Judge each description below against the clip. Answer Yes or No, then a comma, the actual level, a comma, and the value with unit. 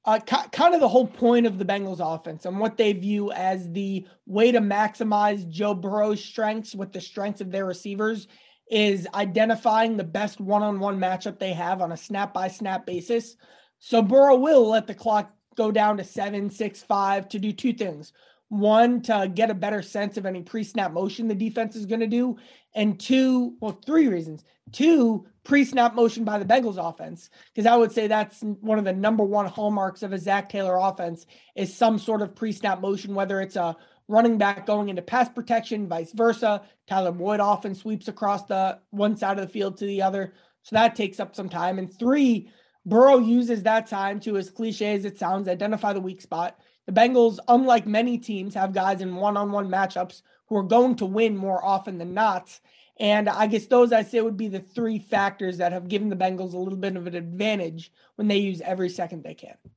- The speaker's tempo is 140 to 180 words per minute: No, fast, 205 wpm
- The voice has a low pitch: No, high, 210 Hz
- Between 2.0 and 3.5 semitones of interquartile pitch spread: Yes, average, 2.8 semitones